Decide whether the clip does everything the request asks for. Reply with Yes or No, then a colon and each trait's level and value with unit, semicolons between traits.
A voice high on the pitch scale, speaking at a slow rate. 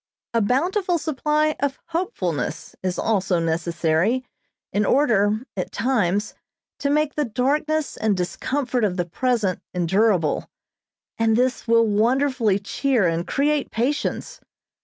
Yes: high, 230 Hz; slow, 120 wpm